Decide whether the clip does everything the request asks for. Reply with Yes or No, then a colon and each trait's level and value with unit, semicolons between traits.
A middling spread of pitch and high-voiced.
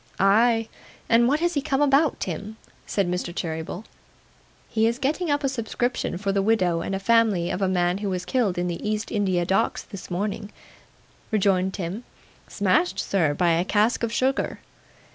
Yes: average, 4.3 semitones; high, 200 Hz